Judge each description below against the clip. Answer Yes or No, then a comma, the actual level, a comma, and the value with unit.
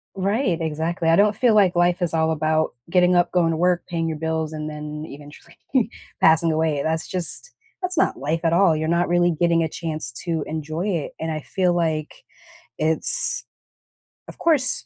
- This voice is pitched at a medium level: Yes, medium, 165 Hz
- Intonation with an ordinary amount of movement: No, narrow, 2.1 semitones